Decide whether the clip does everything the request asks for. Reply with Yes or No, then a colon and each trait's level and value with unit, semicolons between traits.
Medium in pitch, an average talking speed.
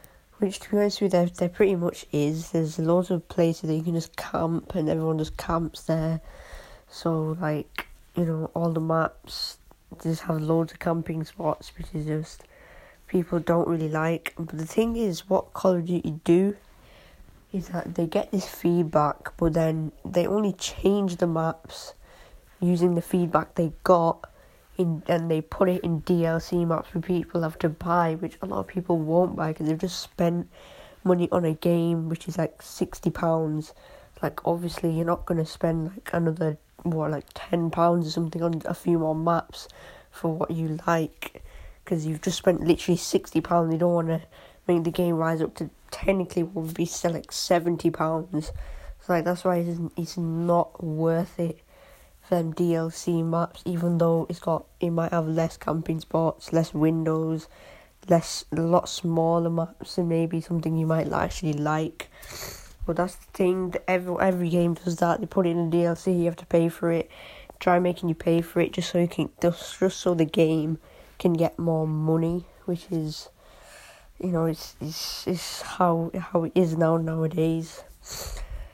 Yes: medium, 170 Hz; average, 185 wpm